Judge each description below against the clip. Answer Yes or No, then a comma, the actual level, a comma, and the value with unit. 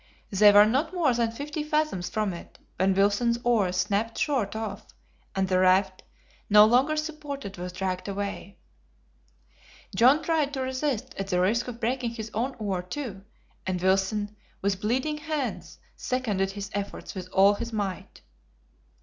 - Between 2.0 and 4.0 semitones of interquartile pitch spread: No, average, 5.2 semitones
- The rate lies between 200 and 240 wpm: No, average, 155 wpm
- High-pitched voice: Yes, high, 215 Hz